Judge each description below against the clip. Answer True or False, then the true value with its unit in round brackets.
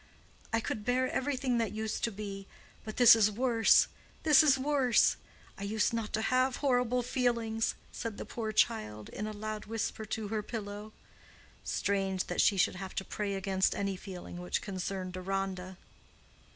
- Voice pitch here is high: True (215 Hz)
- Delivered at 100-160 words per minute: True (155 wpm)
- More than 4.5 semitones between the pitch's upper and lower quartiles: False (3.4 semitones)